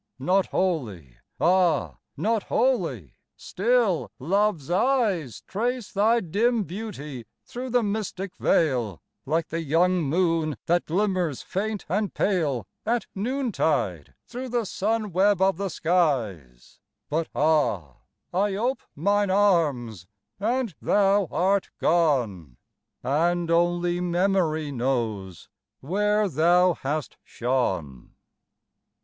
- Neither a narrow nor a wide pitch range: No, wide, 6.3 semitones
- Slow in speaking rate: Yes, slow, 105 wpm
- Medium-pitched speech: Yes, medium, 175 Hz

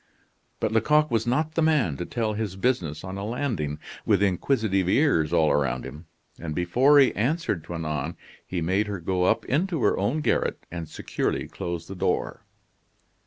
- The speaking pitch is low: Yes, very low, 95 Hz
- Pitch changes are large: Yes, wide, 7.1 semitones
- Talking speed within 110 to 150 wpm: No, average, 170 wpm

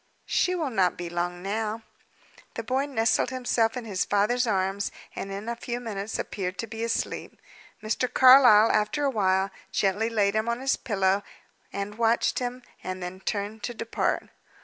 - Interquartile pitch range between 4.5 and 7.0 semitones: No, average, 3.3 semitones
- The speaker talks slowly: No, average, 170 wpm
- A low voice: No, high, 220 Hz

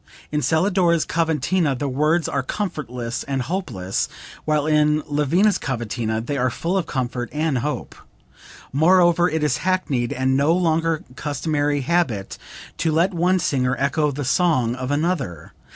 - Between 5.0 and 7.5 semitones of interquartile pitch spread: No, average, 4.4 semitones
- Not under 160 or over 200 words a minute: No, average, 145 wpm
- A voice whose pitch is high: No, medium, 150 Hz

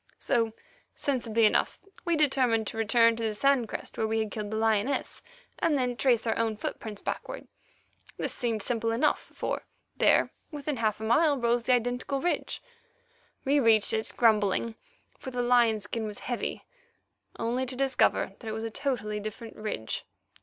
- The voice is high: Yes, high, 230 Hz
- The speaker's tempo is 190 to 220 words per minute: No, average, 170 wpm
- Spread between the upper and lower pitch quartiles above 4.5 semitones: No, average, 2.7 semitones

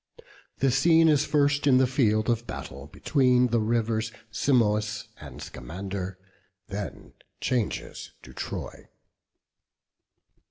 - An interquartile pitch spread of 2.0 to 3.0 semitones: No, average, 4.3 semitones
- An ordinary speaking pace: No, slow, 115 wpm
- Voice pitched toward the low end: Yes, low, 115 Hz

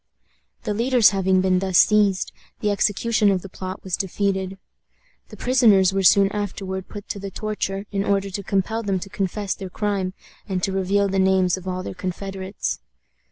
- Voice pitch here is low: No, high, 195 Hz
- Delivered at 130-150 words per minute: No, average, 180 wpm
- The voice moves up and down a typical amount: No, narrow, 1.4 semitones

